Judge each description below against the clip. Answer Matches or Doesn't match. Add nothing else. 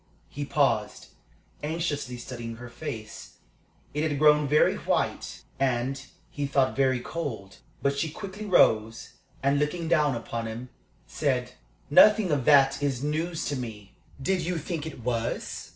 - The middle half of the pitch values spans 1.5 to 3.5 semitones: Doesn't match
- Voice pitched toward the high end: Doesn't match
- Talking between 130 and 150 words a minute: Matches